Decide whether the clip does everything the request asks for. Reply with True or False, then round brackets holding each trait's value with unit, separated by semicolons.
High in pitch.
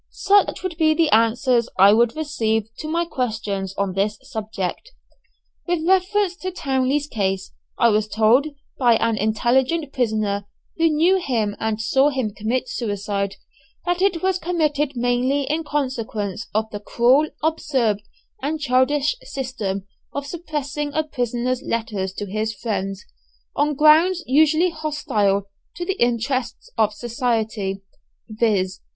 True (250 Hz)